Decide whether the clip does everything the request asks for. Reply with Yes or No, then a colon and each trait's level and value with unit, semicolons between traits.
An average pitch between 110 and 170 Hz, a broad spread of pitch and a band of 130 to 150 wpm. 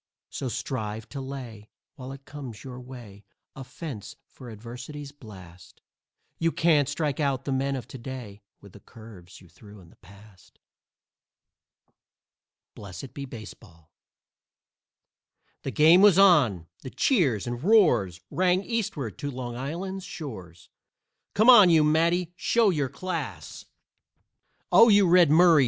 Yes: low, 135 Hz; wide, 7.2 semitones; average, 140 wpm